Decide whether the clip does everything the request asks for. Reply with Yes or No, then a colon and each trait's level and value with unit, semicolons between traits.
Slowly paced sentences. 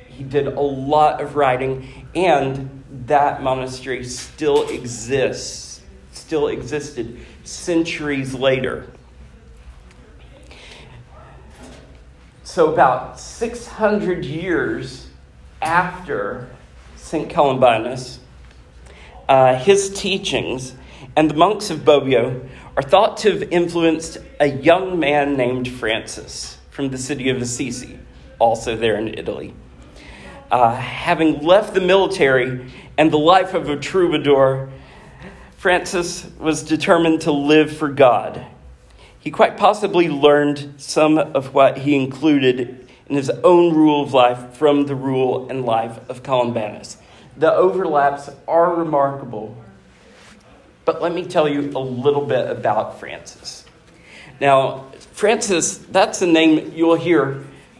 Yes: slow, 115 wpm